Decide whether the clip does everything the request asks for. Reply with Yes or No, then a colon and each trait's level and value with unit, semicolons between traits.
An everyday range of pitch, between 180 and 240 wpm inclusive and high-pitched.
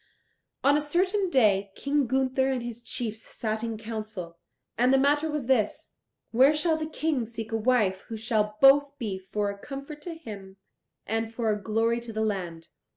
Yes: average, 4.6 semitones; average, 185 wpm; high, 235 Hz